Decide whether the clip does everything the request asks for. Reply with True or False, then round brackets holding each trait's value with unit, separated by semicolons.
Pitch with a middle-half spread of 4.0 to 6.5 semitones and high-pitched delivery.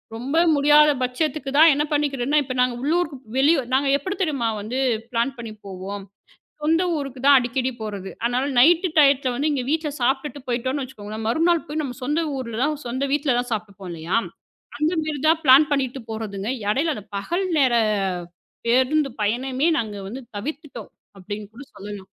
True (4.4 semitones; 265 Hz)